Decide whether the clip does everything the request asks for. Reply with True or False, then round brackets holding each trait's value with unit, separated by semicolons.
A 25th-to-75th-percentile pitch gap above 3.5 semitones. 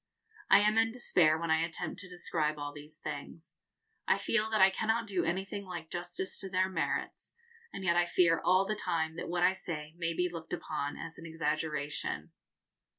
False (3.0 semitones)